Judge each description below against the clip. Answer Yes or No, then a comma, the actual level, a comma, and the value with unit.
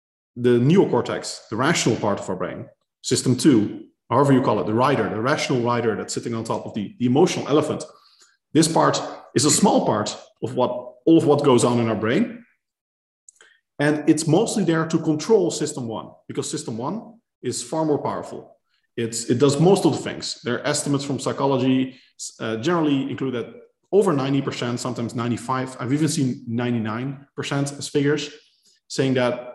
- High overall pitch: No, medium, 140 Hz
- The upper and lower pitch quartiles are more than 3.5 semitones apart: Yes, average, 4.2 semitones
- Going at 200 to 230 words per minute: No, average, 175 wpm